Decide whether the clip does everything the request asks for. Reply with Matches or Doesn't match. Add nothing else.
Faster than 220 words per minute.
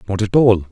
Matches